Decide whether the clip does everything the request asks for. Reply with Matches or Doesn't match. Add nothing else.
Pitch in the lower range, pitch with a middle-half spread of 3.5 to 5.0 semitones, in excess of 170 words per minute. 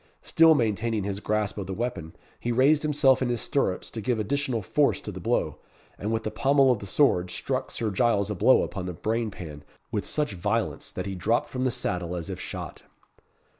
Matches